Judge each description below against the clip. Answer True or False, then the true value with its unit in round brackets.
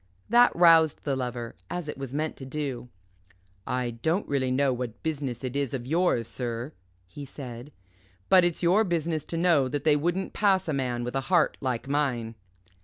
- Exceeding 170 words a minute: True (185 wpm)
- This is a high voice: False (140 Hz)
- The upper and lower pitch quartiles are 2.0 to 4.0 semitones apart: False (4.7 semitones)